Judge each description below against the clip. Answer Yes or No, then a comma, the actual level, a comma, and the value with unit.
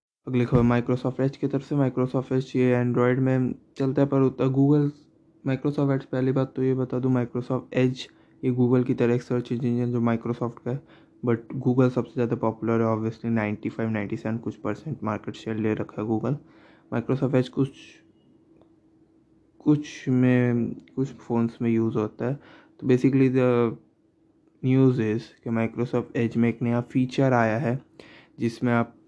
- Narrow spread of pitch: Yes, narrow, 2.1 semitones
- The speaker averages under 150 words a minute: No, average, 170 wpm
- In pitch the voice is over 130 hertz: No, low, 125 Hz